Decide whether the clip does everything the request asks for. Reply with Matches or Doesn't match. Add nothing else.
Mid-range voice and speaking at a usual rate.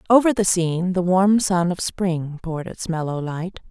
Matches